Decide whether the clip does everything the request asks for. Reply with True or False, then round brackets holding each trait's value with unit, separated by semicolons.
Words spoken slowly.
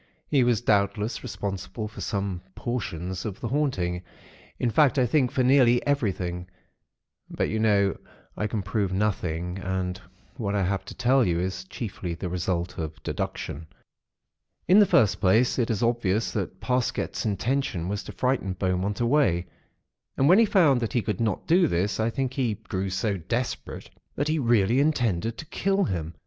False (170 wpm)